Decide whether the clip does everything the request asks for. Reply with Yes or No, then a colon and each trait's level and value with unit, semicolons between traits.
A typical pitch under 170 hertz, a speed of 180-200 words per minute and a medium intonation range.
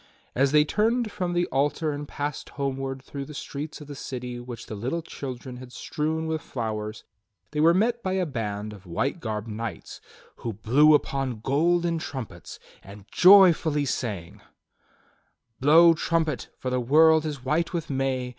No: medium, 140 Hz; average, 165 wpm; average, 4.7 semitones